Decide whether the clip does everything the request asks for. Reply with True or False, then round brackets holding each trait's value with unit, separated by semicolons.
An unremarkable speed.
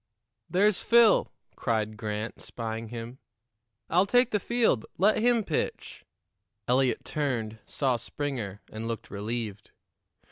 False (115 wpm)